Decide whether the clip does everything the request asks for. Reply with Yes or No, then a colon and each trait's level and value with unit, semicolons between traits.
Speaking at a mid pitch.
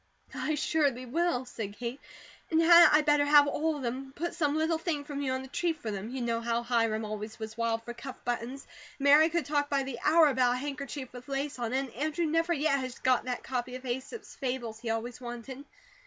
No: very high, 265 Hz